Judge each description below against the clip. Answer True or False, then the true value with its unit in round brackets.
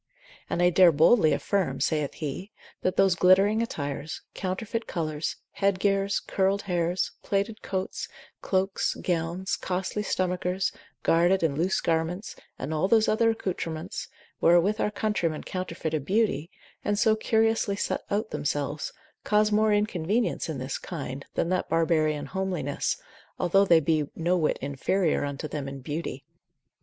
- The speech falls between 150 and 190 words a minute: False (140 wpm)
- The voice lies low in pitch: False (180 Hz)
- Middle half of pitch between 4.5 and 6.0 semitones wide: False (4.1 semitones)